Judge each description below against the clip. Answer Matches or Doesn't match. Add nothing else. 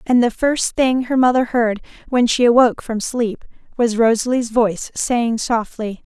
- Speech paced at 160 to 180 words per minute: Matches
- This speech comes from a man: Doesn't match